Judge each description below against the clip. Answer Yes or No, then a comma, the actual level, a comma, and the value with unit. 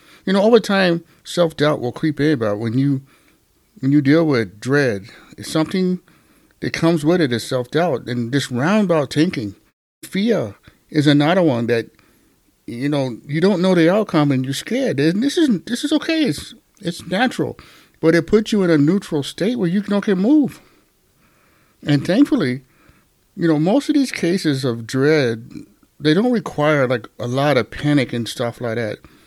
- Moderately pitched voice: Yes, medium, 155 Hz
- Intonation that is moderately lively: No, wide, 6.0 semitones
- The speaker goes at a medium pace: Yes, average, 180 wpm